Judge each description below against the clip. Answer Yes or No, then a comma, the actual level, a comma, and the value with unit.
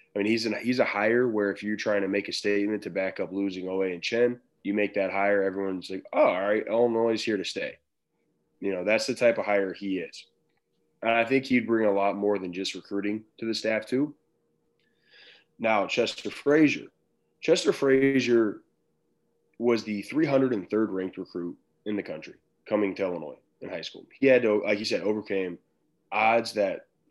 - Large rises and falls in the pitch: No, average, 3.0 semitones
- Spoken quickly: No, average, 195 wpm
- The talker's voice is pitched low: Yes, low, 105 Hz